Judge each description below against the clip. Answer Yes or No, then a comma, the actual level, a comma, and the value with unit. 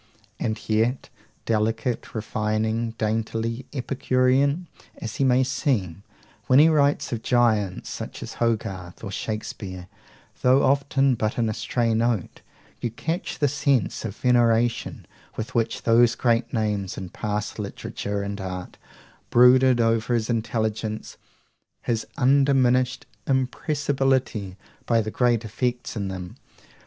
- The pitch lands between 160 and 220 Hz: No, low, 115 Hz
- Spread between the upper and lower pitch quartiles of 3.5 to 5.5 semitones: No, average, 2.9 semitones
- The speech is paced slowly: Yes, slow, 125 wpm